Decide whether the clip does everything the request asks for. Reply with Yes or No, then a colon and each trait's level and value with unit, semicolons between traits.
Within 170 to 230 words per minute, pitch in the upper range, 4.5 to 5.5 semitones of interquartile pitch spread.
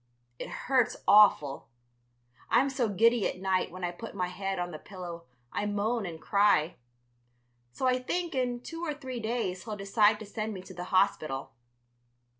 Yes: average, 175 wpm; high, 205 Hz; average, 4.9 semitones